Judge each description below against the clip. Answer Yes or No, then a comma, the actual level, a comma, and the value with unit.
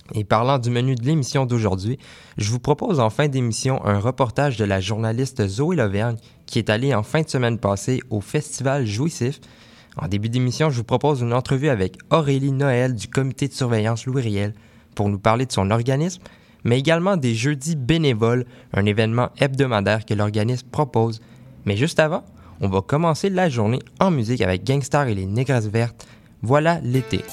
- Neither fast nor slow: Yes, average, 180 wpm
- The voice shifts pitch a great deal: No, average, 4.1 semitones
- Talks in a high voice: No, low, 125 Hz